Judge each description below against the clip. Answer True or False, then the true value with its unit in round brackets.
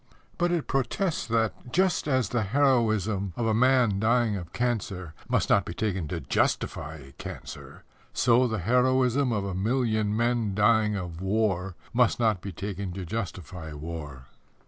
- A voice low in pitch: True (110 Hz)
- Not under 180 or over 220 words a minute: False (155 wpm)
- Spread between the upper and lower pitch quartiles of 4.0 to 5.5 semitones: True (4.6 semitones)